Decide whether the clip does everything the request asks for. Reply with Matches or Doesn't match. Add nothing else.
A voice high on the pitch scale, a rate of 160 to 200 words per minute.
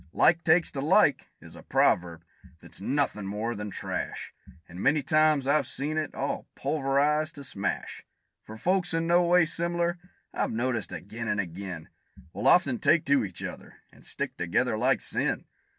Doesn't match